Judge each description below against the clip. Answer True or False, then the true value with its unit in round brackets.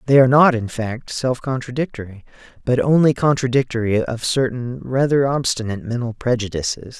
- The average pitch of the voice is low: True (125 Hz)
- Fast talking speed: False (135 wpm)